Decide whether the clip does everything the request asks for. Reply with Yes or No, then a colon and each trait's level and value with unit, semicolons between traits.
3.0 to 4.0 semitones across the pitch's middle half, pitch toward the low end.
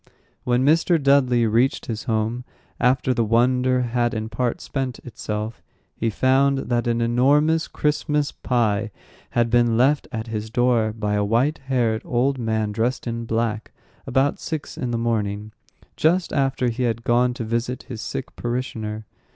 No: narrow, 2.5 semitones; low, 120 Hz